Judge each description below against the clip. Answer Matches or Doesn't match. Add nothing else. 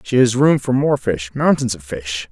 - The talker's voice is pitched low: Matches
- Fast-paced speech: Matches